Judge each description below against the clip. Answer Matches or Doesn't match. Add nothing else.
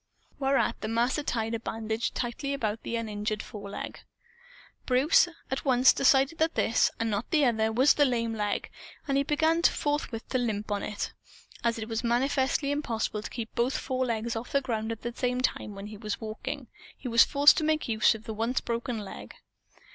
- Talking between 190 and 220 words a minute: Matches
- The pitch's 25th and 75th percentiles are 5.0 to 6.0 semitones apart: Doesn't match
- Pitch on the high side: Matches